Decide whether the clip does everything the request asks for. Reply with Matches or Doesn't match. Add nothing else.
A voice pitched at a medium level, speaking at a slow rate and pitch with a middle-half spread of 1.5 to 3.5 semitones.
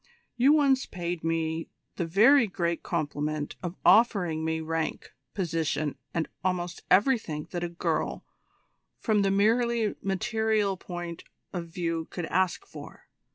Doesn't match